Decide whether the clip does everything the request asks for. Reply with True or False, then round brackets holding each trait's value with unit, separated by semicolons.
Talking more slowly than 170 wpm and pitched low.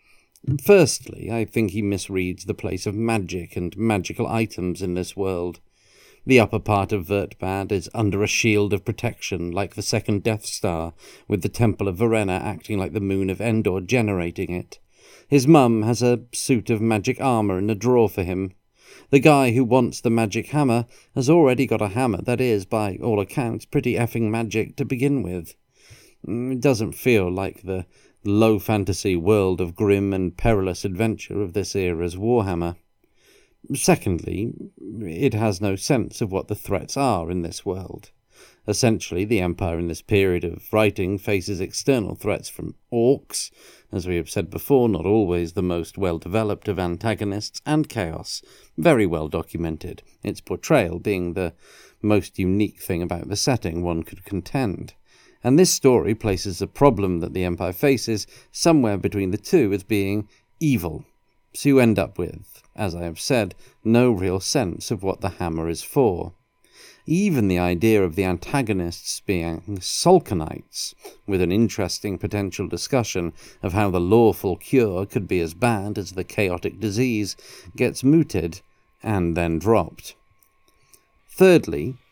True (160 wpm; 105 Hz)